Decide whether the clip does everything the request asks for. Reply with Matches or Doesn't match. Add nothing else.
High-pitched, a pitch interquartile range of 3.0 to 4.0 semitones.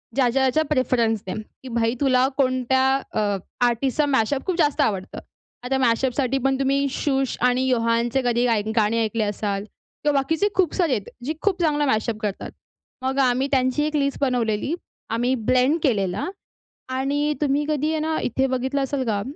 Matches